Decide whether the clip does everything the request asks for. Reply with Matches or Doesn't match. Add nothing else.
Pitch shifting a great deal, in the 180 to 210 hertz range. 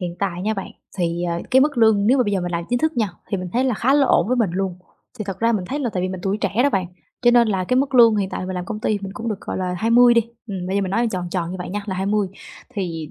Doesn't match